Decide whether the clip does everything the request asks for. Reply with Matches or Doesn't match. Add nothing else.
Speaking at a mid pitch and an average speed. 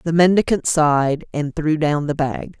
Matches